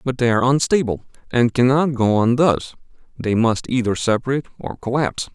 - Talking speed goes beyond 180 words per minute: No, average, 170 wpm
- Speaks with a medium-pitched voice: No, low, 125 Hz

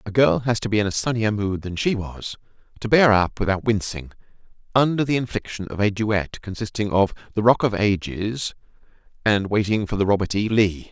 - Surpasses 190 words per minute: Yes, average, 200 wpm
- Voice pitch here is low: Yes, low, 105 Hz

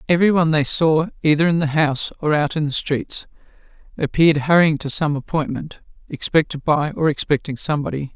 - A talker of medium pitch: Yes, medium, 150 Hz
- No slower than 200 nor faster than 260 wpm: No, average, 170 wpm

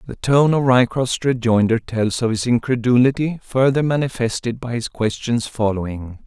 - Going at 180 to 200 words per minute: No, average, 145 wpm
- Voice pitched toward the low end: Yes, low, 120 Hz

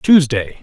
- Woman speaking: No, male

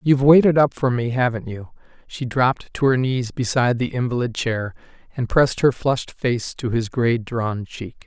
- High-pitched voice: No, low, 125 Hz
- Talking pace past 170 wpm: Yes, average, 195 wpm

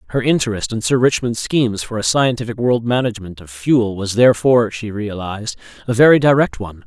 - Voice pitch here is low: Yes, low, 115 Hz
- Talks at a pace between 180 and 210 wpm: Yes, average, 185 wpm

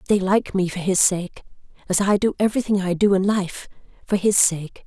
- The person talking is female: Yes, female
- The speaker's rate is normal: No, fast, 210 wpm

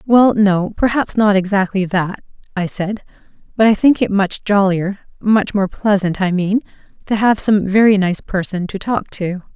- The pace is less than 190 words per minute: Yes, average, 165 wpm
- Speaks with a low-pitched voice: No, high, 200 Hz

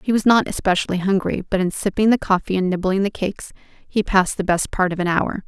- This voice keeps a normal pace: No, fast, 240 wpm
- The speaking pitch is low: No, high, 195 Hz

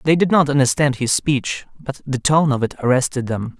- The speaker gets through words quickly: Yes, fast, 215 wpm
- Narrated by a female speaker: No, male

